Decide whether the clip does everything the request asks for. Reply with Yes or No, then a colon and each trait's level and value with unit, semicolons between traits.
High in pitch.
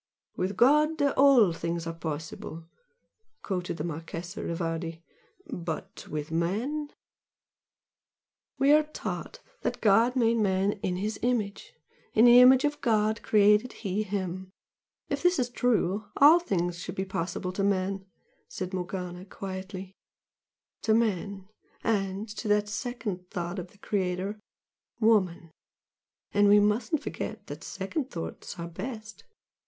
Yes: high, 200 Hz